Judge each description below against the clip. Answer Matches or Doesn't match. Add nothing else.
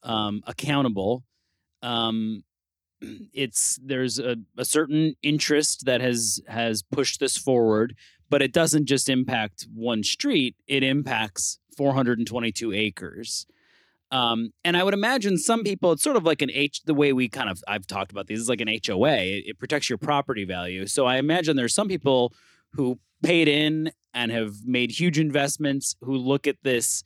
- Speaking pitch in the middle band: Doesn't match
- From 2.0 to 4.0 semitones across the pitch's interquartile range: Doesn't match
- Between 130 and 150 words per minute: Doesn't match